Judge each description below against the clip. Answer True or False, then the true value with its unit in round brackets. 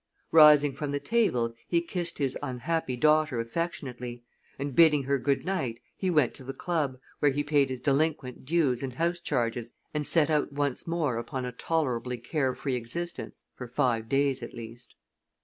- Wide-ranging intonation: False (3.8 semitones)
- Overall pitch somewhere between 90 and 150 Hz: True (140 Hz)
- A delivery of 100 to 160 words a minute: False (175 wpm)